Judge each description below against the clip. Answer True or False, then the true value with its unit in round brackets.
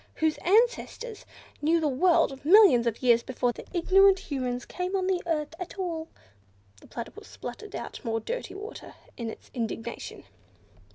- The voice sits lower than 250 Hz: False (330 Hz)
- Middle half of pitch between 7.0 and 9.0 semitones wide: True (7.6 semitones)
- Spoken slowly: False (155 wpm)